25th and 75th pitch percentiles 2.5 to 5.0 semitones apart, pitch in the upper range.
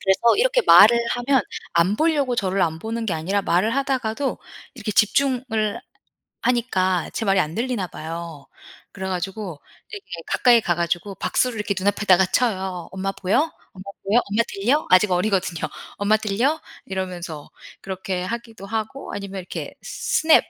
Yes: average, 4.3 semitones; high, 205 Hz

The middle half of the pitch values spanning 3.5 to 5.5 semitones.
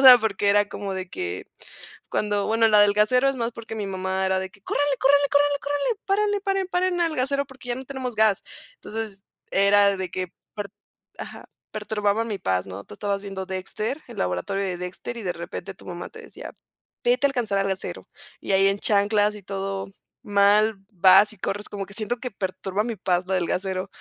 Yes: average, 4.1 semitones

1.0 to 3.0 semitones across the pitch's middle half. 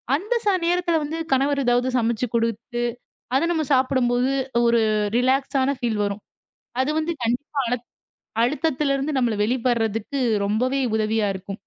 No: average, 3.4 semitones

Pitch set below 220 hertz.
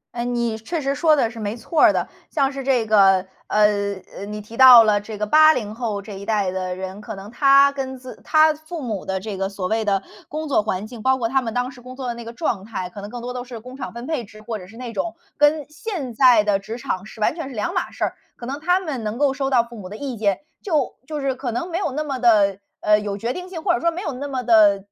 No: high, 235 Hz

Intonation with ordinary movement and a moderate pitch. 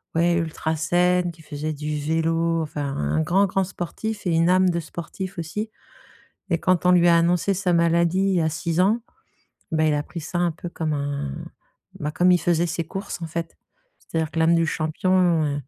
No: narrow, 2.2 semitones; medium, 170 Hz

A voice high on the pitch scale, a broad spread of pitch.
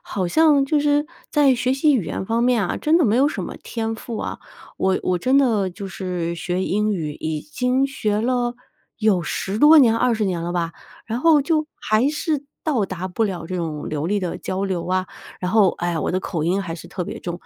Yes: high, 210 Hz; wide, 6.2 semitones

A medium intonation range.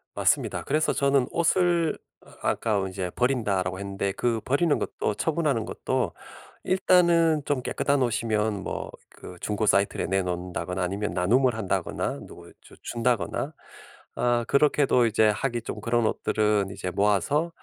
No: wide, 5.9 semitones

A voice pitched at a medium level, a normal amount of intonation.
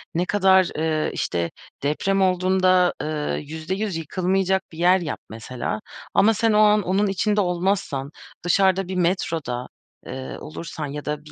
Yes: medium, 180 Hz; average, 3.9 semitones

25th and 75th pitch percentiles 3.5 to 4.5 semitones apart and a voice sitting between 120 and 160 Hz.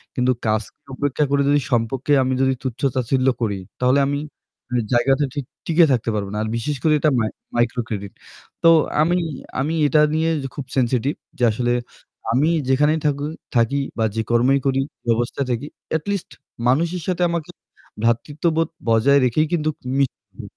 Yes: average, 4.0 semitones; low, 135 Hz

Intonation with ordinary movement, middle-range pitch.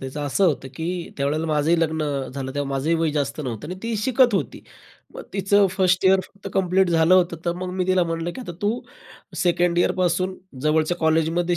Yes: average, 3.2 semitones; medium, 170 Hz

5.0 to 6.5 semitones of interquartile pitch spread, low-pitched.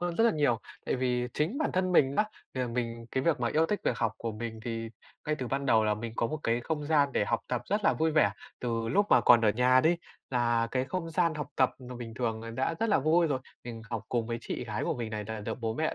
Yes: average, 5.3 semitones; low, 125 Hz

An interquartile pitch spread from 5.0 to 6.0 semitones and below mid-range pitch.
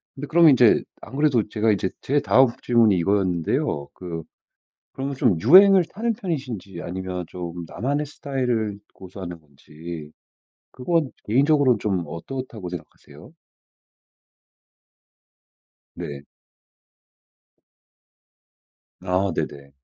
No: wide, 7.6 semitones; low, 105 Hz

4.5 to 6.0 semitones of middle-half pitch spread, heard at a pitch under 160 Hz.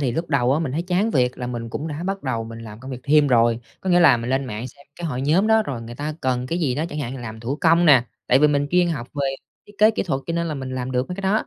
Yes: average, 5.1 semitones; medium, 140 Hz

